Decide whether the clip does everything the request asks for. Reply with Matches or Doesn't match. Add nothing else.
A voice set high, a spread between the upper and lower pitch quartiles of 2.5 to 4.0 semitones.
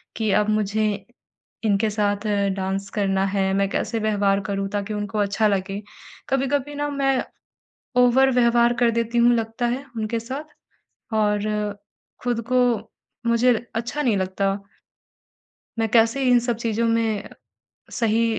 Matches